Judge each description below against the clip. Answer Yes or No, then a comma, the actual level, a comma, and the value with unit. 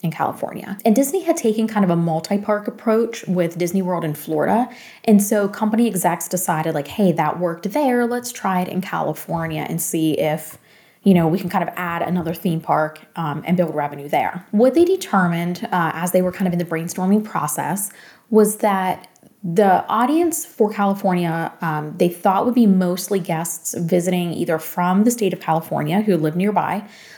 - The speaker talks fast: No, average, 190 wpm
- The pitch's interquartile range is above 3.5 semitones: Yes, average, 4.3 semitones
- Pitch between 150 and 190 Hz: Yes, medium, 185 Hz